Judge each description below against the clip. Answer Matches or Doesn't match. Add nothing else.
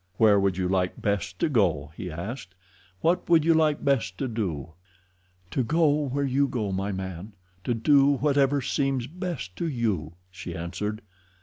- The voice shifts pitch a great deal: Matches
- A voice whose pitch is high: Doesn't match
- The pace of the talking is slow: Doesn't match